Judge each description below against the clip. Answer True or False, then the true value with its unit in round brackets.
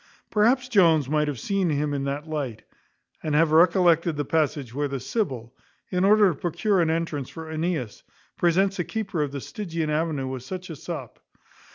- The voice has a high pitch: False (160 Hz)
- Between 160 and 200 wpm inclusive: True (185 wpm)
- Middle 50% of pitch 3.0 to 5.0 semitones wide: True (4.0 semitones)